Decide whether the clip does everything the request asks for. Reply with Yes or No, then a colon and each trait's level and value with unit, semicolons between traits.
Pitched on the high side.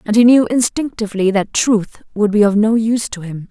Yes: high, 215 Hz